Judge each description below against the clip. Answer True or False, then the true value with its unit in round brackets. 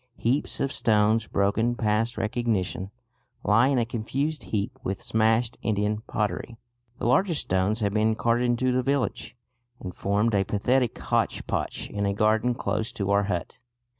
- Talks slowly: False (155 wpm)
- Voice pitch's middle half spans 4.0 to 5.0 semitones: False (2.8 semitones)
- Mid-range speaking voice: False (110 Hz)